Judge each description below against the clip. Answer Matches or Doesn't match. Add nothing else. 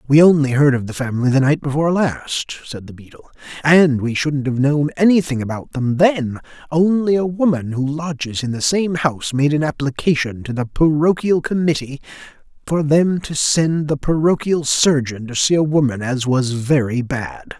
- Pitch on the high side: Doesn't match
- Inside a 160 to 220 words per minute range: Matches